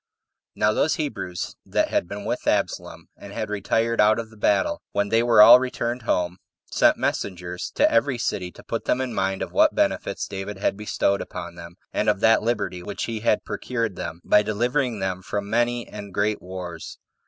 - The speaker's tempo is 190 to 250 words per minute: Yes, average, 200 wpm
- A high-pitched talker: No, low, 105 Hz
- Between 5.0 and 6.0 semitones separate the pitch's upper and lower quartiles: No, average, 3.4 semitones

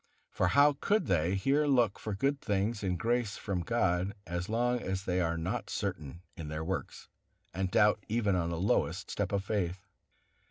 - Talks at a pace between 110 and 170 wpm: No, average, 185 wpm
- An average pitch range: Yes, average, 4.4 semitones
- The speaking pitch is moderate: No, low, 100 Hz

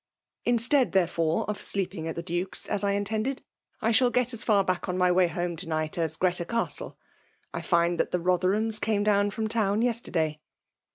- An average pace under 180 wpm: No, average, 195 wpm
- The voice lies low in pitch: No, high, 195 Hz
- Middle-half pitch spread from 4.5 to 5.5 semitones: No, average, 4.0 semitones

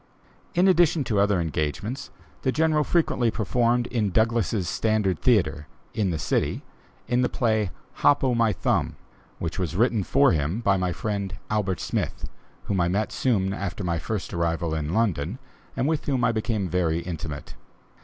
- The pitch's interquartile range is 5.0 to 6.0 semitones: Yes, average, 5.3 semitones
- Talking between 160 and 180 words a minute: Yes, average, 165 wpm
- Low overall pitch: Yes, low, 105 Hz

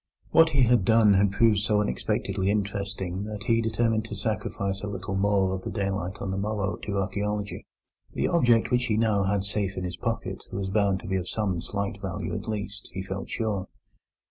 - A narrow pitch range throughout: Yes, narrow, 2.0 semitones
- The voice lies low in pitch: Yes, low, 100 Hz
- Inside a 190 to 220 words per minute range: Yes, average, 200 wpm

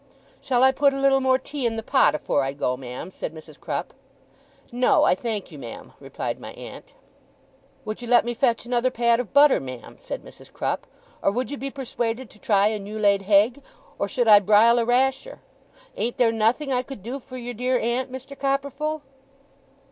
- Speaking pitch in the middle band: No, high, 240 Hz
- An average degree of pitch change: Yes, average, 3.8 semitones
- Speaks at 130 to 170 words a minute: No, average, 200 wpm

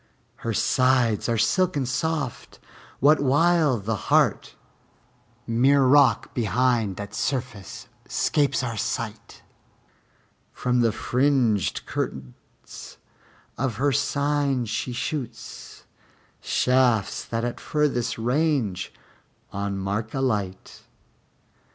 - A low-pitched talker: Yes, low, 125 Hz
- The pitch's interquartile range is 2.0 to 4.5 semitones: Yes, average, 4.1 semitones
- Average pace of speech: No, slow, 95 wpm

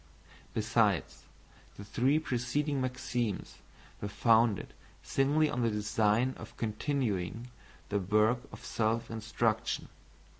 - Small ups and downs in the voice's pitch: No, average, 3.1 semitones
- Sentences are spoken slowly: Yes, slow, 105 wpm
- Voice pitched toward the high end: No, low, 115 Hz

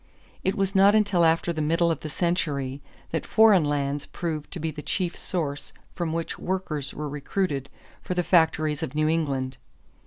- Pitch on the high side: No, medium, 160 Hz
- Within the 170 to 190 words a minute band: Yes, average, 180 wpm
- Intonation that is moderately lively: Yes, average, 3.3 semitones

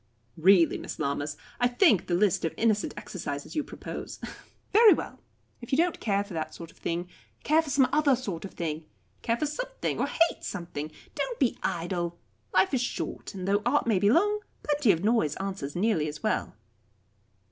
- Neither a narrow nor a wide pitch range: No, wide, 8.7 semitones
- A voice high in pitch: Yes, high, 205 Hz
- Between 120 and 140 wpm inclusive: No, average, 190 wpm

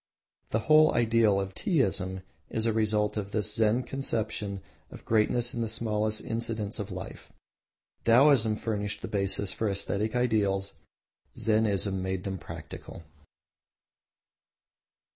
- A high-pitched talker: No, low, 110 Hz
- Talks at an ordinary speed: No, slow, 125 wpm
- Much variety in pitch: No, narrow, 2.5 semitones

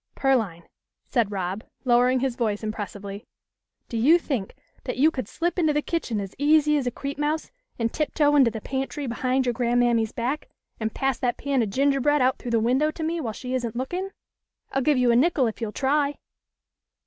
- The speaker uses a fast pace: Yes, fast, 210 wpm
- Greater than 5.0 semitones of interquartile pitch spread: No, average, 4.1 semitones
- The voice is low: No, very high, 255 Hz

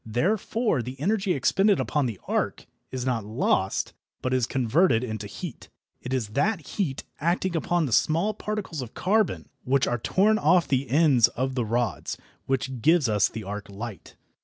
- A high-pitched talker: No, low, 130 Hz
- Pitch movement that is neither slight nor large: No, wide, 7.0 semitones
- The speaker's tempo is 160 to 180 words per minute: Yes, average, 170 wpm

